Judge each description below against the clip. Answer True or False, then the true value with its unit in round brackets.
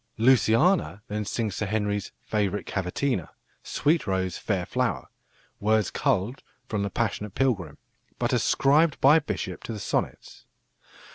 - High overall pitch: False (105 Hz)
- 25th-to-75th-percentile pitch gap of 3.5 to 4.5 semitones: False (5.1 semitones)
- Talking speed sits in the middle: False (130 wpm)